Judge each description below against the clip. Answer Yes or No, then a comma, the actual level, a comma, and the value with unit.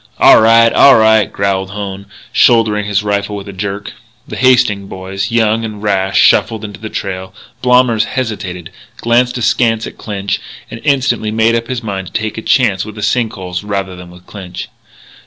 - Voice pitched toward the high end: No, low, 105 Hz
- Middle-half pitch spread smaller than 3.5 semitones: Yes, average, 2.8 semitones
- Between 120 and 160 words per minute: No, average, 180 wpm